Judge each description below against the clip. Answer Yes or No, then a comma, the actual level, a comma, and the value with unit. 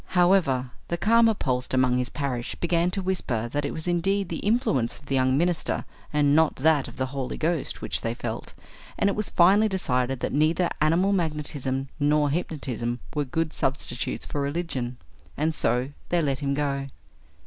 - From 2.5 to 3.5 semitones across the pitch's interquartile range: No, average, 4.7 semitones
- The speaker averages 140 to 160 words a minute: No, average, 180 wpm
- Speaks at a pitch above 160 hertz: No, medium, 150 Hz